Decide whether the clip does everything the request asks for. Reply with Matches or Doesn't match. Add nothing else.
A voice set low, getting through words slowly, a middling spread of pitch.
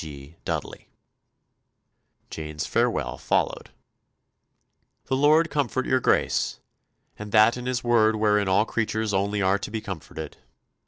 Matches